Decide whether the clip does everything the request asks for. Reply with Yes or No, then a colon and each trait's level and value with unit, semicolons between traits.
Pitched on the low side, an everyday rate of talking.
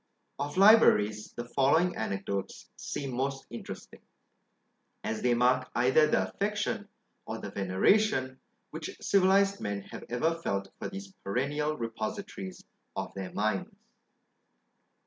No: low, 130 Hz; slow, 120 wpm